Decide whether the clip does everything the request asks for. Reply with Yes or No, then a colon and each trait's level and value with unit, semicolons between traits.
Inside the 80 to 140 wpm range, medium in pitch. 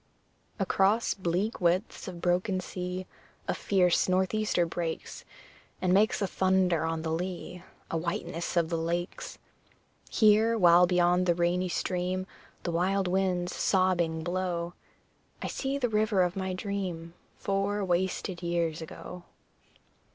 Yes: slow, 135 wpm; medium, 180 Hz